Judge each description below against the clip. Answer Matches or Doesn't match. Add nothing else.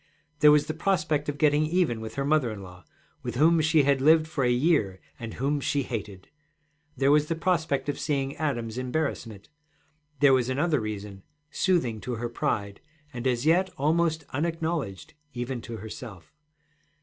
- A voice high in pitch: Doesn't match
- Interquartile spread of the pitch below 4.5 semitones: Doesn't match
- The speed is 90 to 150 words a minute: Doesn't match